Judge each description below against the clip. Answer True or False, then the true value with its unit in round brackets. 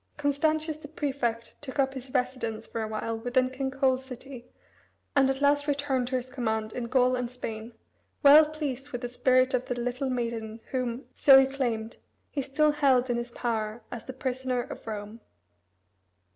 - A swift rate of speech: False (180 wpm)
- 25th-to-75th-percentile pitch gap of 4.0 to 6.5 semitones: False (2.4 semitones)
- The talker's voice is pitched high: True (255 Hz)